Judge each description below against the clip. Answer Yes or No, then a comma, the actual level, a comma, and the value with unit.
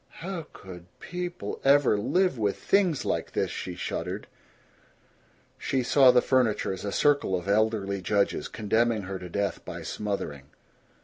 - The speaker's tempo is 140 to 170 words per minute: Yes, average, 145 wpm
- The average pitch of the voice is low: Yes, low, 110 Hz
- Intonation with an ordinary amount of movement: No, wide, 6.1 semitones